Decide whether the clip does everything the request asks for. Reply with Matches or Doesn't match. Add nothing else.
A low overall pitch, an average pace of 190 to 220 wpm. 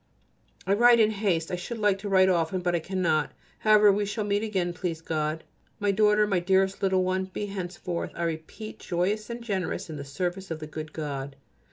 Doesn't match